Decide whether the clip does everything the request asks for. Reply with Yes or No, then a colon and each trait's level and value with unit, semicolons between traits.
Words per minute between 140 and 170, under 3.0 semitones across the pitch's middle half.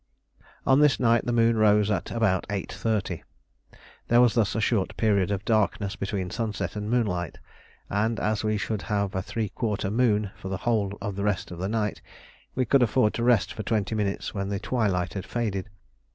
No: average, 195 wpm; narrow, 2.6 semitones